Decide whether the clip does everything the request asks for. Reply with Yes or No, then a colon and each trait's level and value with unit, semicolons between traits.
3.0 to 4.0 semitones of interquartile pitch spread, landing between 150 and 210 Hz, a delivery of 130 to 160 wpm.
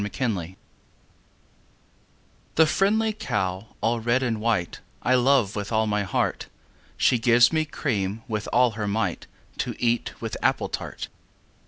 No: average, 3.5 semitones; low, 115 Hz; average, 150 wpm